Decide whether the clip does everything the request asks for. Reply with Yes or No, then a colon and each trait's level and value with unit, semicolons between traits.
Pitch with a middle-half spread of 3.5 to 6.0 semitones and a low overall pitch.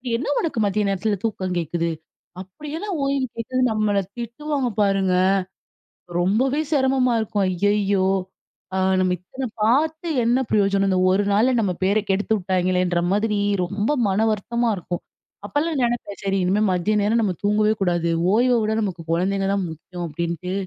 No: average, 4.2 semitones; high, 205 Hz